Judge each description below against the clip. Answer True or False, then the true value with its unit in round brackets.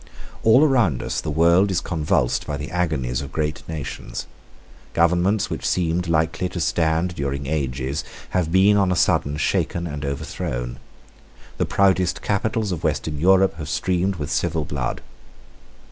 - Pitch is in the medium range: False (80 Hz)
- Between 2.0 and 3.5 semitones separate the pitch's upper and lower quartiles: False (4.1 semitones)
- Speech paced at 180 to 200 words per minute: False (155 wpm)